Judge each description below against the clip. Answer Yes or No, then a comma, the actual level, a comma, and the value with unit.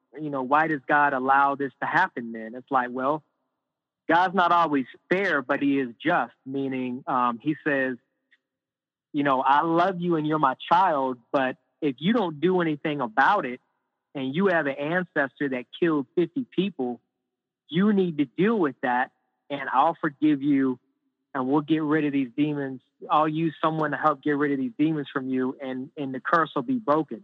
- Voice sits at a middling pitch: Yes, medium, 145 Hz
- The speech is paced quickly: No, average, 190 wpm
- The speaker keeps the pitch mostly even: No, average, 3.1 semitones